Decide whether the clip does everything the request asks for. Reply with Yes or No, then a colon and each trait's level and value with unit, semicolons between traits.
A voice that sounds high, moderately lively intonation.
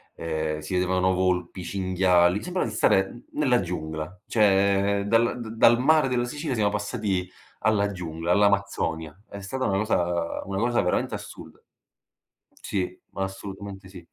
No: very low, 95 Hz; average, 3.2 semitones